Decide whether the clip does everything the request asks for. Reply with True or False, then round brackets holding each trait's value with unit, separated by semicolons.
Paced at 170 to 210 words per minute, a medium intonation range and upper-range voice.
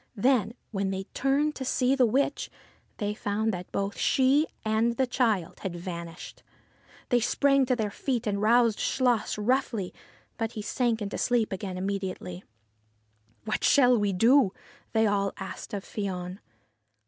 False (160 wpm; 4.4 semitones; 215 Hz)